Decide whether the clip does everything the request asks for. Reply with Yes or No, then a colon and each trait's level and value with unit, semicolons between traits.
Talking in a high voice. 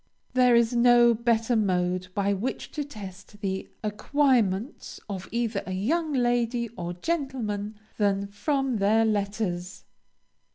Yes: high, 220 Hz